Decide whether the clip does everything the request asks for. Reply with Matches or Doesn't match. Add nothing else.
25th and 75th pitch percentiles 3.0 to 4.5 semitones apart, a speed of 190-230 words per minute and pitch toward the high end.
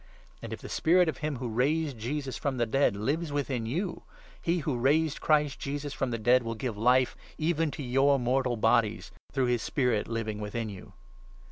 Doesn't match